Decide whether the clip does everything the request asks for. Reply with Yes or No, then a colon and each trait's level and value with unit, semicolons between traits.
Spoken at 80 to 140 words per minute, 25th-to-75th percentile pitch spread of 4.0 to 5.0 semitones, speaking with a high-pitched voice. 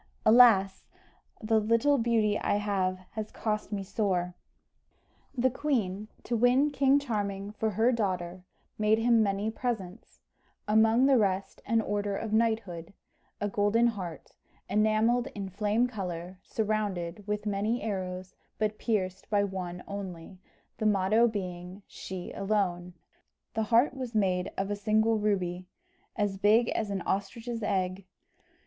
No: slow, 135 wpm; average, 2.9 semitones; high, 210 Hz